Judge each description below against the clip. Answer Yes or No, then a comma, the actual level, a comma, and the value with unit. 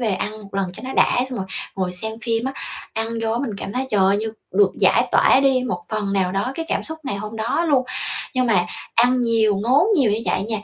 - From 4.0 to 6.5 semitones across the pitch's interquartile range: Yes, average, 4.3 semitones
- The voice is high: Yes, high, 225 Hz